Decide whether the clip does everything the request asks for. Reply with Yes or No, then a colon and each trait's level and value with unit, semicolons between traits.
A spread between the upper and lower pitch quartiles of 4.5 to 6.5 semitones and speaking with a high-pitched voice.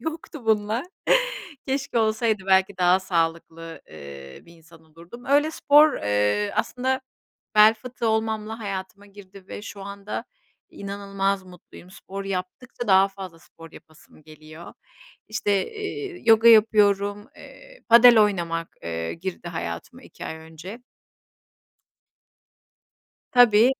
Yes: average, 5.0 semitones; high, 200 Hz